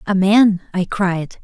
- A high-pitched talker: Yes, high, 195 Hz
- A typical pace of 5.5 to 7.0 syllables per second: No, 3.5 syllables/s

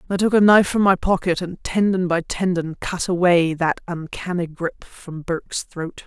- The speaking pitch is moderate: Yes, medium, 180 Hz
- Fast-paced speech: No, average, 190 wpm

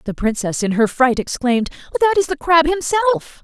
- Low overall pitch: No, very high, 295 Hz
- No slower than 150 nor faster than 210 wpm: Yes, average, 190 wpm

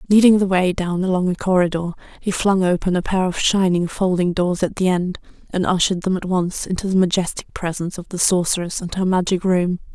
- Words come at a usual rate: No, fast, 210 wpm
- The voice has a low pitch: No, medium, 185 Hz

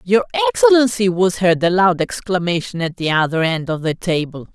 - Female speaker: Yes, female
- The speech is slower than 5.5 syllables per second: Yes, 5.3 syllables/s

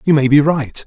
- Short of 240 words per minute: No, fast, 280 wpm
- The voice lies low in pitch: No, medium, 145 Hz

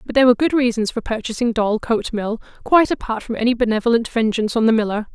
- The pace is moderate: No, fast, 210 wpm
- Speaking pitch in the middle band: No, high, 230 Hz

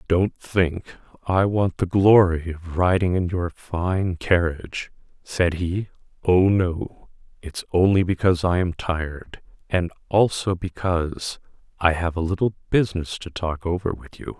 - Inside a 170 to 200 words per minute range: No, average, 145 wpm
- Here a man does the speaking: Yes, male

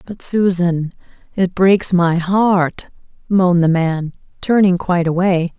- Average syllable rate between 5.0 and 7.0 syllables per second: No, 3.9 syllables/s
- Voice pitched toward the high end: No, medium, 180 Hz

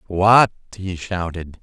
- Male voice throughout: Yes, male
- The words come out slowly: Yes, slow, 110 wpm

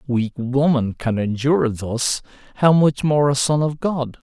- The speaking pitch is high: No, low, 135 Hz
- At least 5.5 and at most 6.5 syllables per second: No, 4.3 syllables/s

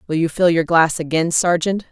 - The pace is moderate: No, fast, 220 wpm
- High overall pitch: No, medium, 165 Hz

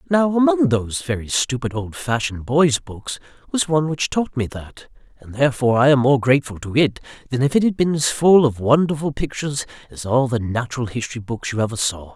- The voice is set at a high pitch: No, low, 135 Hz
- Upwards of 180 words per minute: Yes, average, 200 wpm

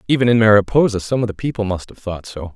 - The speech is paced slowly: No, fast, 260 wpm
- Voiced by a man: Yes, male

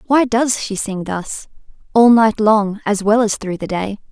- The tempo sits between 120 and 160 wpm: No, fast, 205 wpm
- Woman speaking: Yes, female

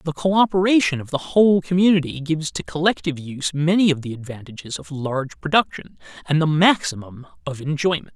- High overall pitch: No, medium, 155 Hz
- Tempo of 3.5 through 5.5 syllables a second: No, 5.9 syllables/s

